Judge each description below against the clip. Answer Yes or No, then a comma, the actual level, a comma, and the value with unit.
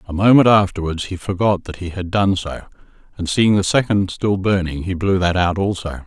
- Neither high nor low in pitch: No, very low, 95 Hz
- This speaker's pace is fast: Yes, fast, 210 wpm